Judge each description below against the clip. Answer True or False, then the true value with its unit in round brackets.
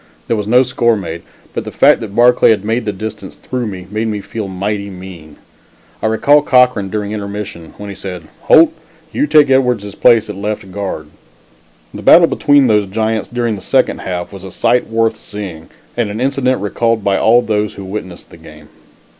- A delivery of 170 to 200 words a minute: True (195 wpm)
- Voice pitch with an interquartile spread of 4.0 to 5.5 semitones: False (3.4 semitones)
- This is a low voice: True (105 Hz)